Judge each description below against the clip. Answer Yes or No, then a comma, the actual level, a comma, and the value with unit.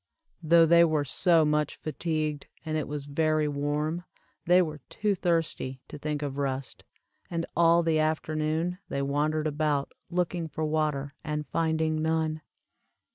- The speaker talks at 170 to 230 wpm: No, average, 145 wpm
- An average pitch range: No, narrow, 1.7 semitones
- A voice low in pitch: No, medium, 155 Hz